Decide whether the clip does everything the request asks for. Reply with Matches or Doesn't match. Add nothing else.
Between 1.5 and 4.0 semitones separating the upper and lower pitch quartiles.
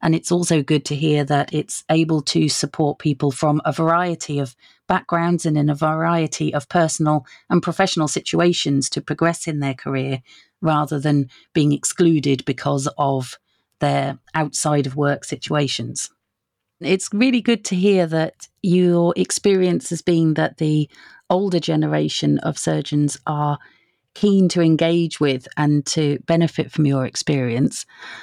Matches